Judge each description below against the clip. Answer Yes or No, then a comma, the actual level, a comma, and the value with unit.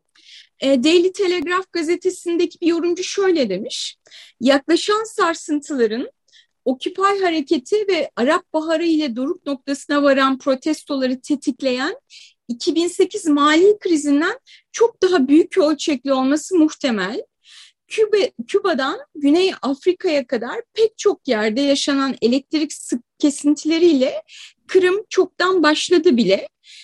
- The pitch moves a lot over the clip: No, average, 4.7 semitones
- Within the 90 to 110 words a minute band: Yes, average, 100 wpm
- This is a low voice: No, very high, 320 Hz